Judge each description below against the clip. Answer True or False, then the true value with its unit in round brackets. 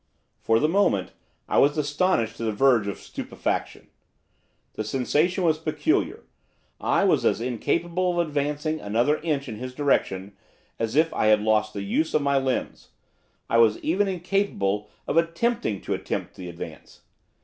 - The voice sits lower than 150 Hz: True (140 Hz)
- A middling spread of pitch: False (7.0 semitones)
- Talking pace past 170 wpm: False (160 wpm)